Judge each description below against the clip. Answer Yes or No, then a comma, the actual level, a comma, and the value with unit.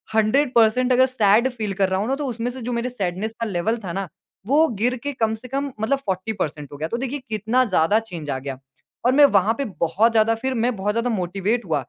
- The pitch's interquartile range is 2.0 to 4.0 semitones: No, average, 4.8 semitones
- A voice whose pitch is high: Yes, high, 220 Hz